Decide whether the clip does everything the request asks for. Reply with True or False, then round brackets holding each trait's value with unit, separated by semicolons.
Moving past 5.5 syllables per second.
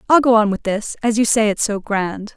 False (5.2 syllables/s)